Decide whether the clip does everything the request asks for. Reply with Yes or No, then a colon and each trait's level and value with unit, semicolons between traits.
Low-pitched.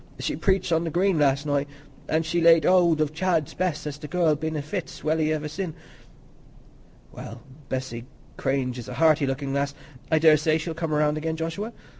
No: medium, 155 Hz